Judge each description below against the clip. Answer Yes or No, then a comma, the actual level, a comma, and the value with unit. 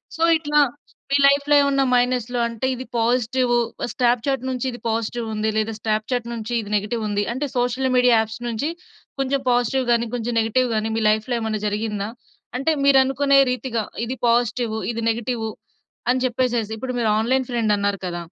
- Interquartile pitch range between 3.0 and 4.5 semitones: No, narrow, 2.6 semitones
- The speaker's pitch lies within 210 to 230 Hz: No, high, 240 Hz